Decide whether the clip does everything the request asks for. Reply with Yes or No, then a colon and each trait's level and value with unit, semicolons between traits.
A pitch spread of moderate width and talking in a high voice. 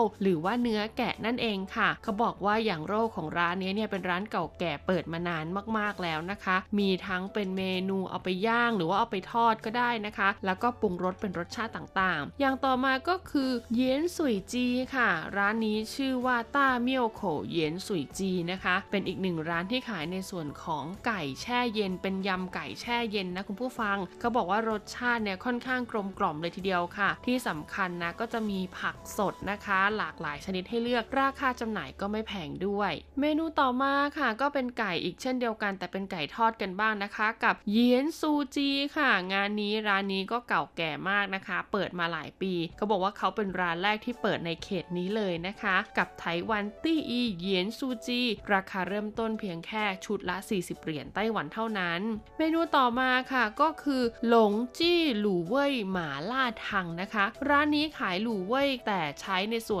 Yes: average, 4.3 semitones; high, 210 Hz